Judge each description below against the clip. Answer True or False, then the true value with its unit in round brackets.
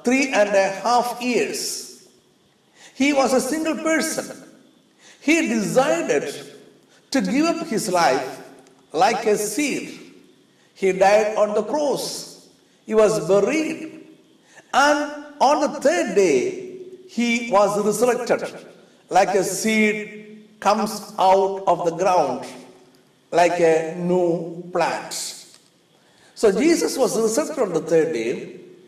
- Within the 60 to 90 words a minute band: False (115 wpm)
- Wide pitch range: True (7.5 semitones)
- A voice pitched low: False (220 Hz)